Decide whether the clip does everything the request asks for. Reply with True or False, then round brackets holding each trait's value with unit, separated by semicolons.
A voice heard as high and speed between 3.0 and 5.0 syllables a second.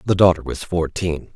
False (85 Hz; 4.9 syllables/s)